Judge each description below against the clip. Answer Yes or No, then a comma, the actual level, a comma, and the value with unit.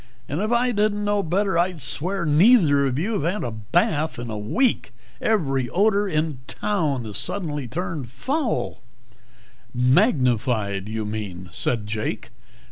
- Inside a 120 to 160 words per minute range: Yes, average, 150 wpm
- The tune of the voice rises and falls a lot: Yes, wide, 8.8 semitones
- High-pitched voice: No, medium, 150 Hz